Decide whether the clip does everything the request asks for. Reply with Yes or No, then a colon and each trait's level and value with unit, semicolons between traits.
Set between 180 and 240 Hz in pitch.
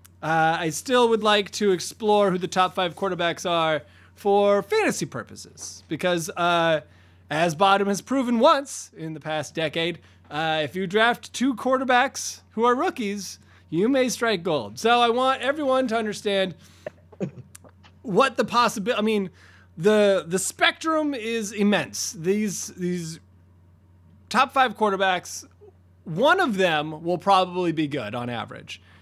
Yes: high, 190 Hz